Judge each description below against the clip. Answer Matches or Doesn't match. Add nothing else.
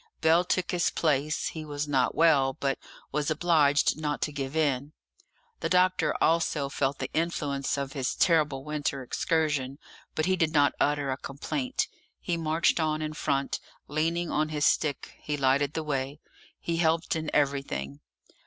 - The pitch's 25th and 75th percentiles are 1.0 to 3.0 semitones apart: Matches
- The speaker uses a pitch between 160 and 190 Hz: Doesn't match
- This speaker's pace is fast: Doesn't match